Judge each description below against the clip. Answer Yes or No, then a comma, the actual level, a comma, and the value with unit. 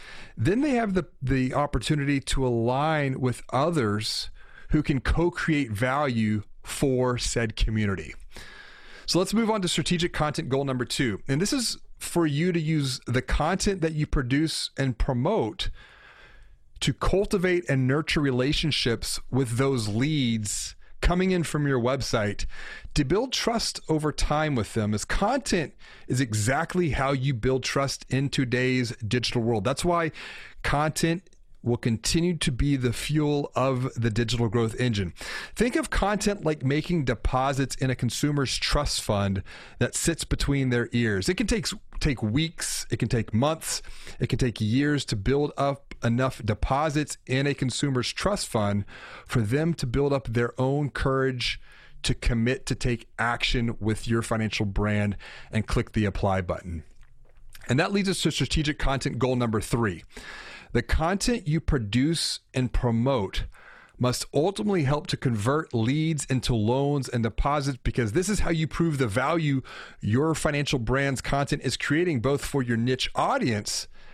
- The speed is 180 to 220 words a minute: No, average, 155 wpm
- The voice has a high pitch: No, low, 135 Hz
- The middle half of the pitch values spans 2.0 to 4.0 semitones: No, average, 4.4 semitones